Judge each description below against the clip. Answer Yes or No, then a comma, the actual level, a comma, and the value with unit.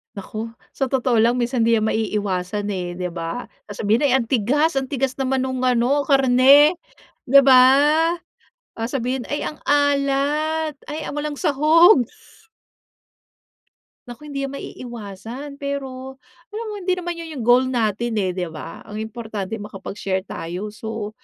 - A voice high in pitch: Yes, very high, 255 Hz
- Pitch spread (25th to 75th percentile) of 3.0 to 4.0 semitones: No, average, 4.7 semitones